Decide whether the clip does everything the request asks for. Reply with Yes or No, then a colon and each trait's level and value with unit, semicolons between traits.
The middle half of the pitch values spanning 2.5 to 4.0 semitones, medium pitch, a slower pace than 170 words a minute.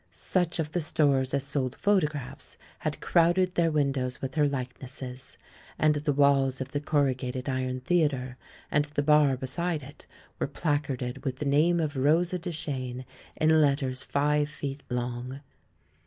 Yes: average, 2.9 semitones; medium, 145 Hz; average, 155 wpm